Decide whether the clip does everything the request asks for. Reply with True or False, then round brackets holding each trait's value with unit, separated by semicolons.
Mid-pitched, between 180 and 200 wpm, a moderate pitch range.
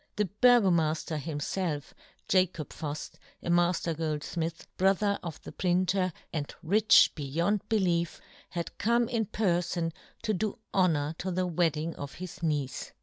False (175 Hz; 135 wpm; 3.3 semitones)